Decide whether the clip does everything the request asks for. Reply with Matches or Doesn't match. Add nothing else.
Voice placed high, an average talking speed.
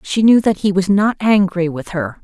Doesn't match